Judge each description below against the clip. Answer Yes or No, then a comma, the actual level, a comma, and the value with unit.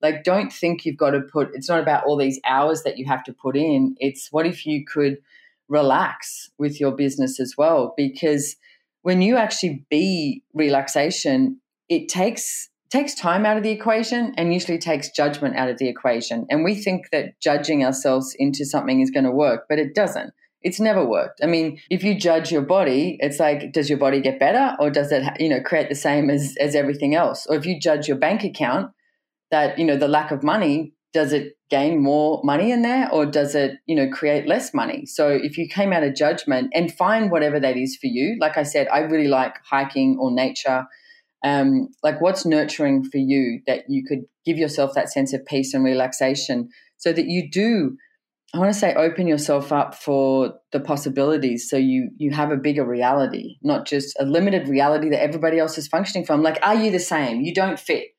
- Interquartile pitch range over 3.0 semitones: Yes, average, 4.8 semitones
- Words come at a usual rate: No, fast, 210 wpm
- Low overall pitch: No, medium, 150 Hz